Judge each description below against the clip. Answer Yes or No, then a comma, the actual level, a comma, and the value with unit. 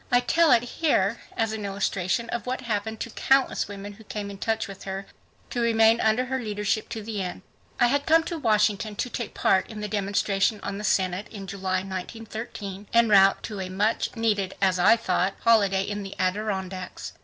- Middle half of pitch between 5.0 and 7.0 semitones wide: No, average, 2.7 semitones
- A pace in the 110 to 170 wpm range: No, average, 195 wpm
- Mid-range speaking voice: No, high, 210 Hz